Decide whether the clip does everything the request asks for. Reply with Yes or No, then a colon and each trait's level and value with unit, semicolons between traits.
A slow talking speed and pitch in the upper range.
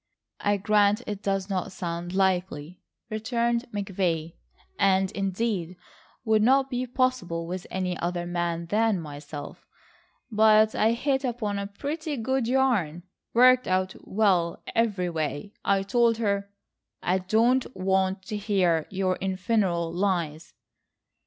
Yes: slow, 120 wpm; high, 195 Hz